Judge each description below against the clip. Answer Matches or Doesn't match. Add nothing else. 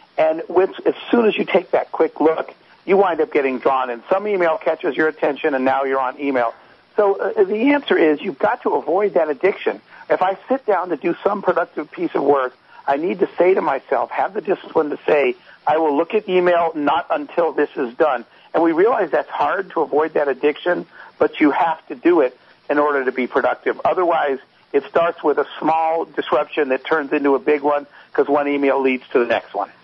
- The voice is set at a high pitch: Doesn't match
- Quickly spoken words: Matches